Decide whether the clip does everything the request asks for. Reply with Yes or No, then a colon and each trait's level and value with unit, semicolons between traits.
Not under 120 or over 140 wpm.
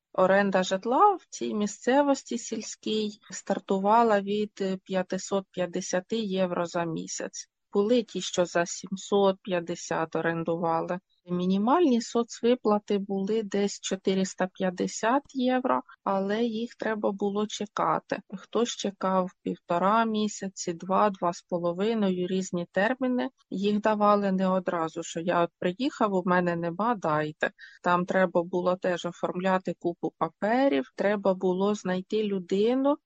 No: average, 110 wpm